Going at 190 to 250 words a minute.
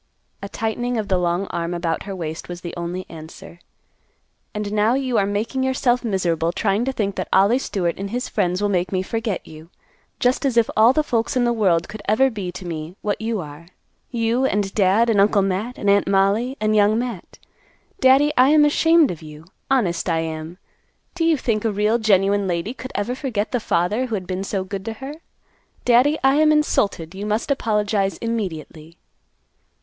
Yes: average, 200 wpm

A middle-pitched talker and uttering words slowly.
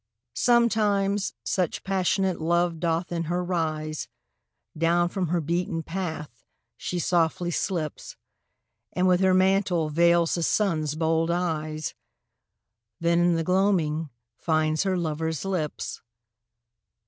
Yes: medium, 170 Hz; slow, 115 wpm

